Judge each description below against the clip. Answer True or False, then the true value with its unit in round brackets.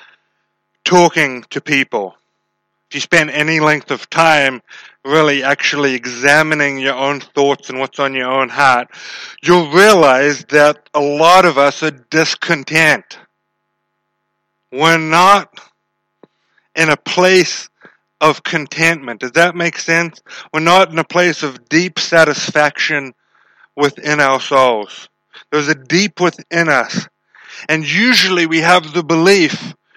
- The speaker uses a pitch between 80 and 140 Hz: False (155 Hz)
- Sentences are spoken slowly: True (130 wpm)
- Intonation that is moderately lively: True (3.0 semitones)